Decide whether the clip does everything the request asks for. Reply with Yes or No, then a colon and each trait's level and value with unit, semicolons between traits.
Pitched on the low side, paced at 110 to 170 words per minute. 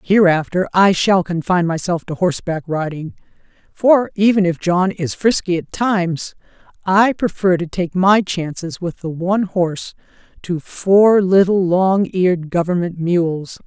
No: medium, 180 Hz; average, 140 wpm